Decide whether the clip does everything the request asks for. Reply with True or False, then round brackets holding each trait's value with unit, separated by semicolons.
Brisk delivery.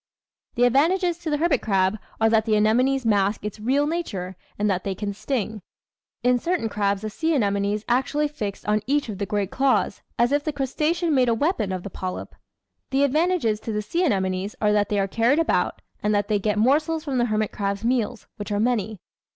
True (215 wpm)